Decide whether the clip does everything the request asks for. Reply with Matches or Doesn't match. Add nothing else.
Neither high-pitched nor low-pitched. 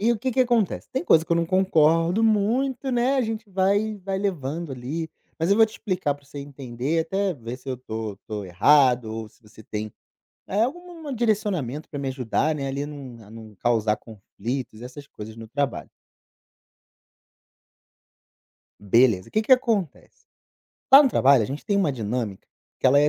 Matches